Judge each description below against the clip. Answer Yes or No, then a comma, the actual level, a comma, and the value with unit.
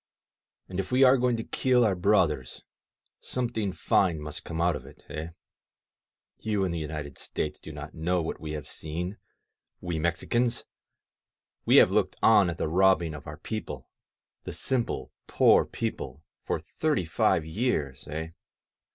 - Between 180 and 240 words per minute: No, average, 160 wpm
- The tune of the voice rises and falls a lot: Yes, wide, 5.7 semitones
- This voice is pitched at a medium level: No, very low, 85 Hz